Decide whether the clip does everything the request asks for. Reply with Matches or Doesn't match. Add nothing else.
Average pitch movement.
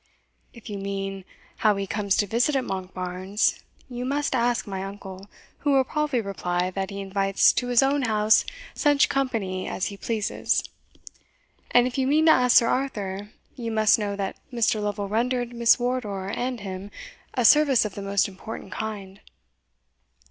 Matches